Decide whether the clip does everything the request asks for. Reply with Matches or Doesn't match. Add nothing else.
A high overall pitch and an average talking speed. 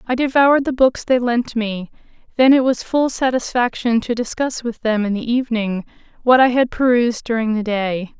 Matches